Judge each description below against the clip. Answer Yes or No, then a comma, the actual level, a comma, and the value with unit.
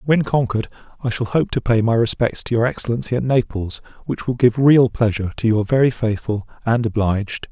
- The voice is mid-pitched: No, low, 115 Hz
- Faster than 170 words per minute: Yes, average, 200 wpm